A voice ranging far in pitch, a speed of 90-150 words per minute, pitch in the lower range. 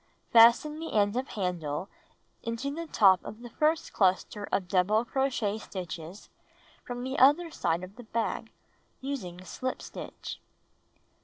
No: wide, 6.0 semitones; average, 140 wpm; high, 220 Hz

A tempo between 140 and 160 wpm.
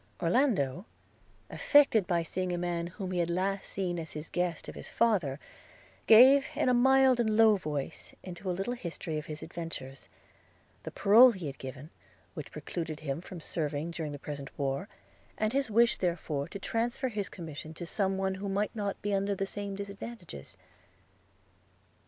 No: average, 175 wpm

